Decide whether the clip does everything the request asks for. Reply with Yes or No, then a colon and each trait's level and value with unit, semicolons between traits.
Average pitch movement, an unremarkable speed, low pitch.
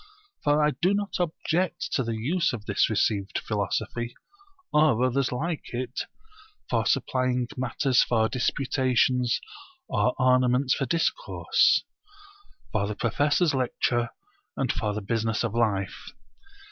No: average, 4.1 semitones; slow, 125 wpm; low, 125 Hz